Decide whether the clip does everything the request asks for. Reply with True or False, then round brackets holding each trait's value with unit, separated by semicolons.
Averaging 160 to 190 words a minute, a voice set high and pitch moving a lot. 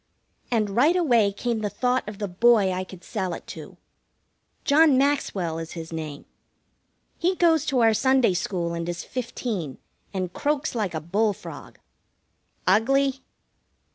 False (150 wpm; 215 Hz; 6.4 semitones)